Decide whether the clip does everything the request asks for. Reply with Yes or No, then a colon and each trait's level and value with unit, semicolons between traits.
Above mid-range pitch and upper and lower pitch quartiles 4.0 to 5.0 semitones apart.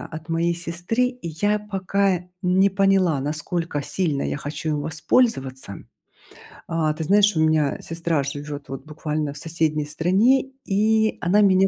No: medium, 165 Hz; average, 4.5 semitones